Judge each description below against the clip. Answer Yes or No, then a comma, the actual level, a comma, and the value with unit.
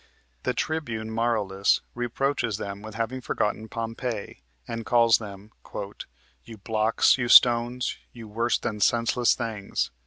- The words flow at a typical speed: No, slow, 125 wpm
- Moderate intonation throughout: No, narrow, 1.9 semitones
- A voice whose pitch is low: Yes, low, 115 Hz